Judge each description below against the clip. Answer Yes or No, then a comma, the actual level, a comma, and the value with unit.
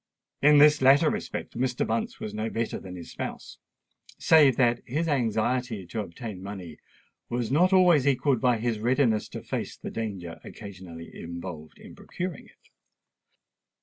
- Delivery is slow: No, average, 150 wpm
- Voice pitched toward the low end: Yes, low, 115 Hz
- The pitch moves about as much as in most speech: No, wide, 5.7 semitones